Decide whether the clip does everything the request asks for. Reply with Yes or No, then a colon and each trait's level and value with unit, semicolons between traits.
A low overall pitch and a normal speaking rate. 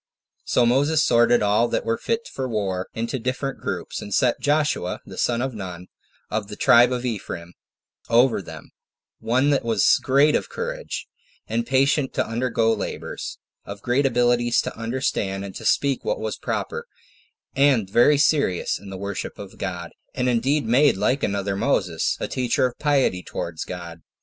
Yes: low, 120 Hz; average, 170 wpm